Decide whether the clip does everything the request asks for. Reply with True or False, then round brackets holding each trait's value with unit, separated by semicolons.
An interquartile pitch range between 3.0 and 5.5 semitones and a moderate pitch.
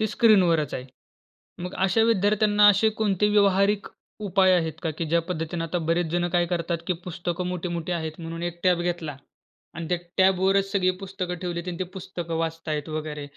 False (2.5 semitones; 175 Hz)